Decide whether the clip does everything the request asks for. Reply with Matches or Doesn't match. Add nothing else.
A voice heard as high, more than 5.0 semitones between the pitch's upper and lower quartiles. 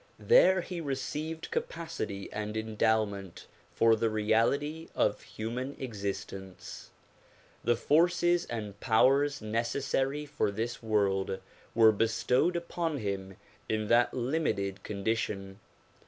Doesn't match